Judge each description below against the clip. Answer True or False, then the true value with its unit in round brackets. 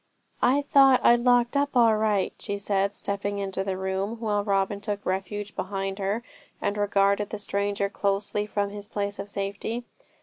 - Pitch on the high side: True (205 Hz)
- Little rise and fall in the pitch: True (1.5 semitones)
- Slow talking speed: False (170 wpm)